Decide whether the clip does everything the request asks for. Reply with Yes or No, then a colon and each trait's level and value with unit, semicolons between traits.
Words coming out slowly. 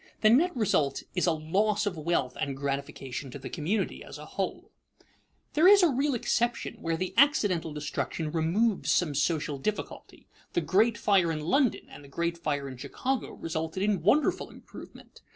No: average, 170 wpm